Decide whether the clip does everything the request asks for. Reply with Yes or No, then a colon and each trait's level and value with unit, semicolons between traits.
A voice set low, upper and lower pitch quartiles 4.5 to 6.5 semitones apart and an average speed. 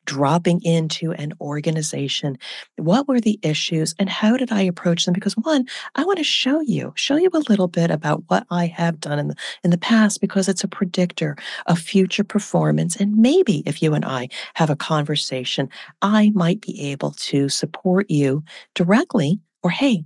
No: medium, 175 Hz; average, 4.9 semitones; average, 185 wpm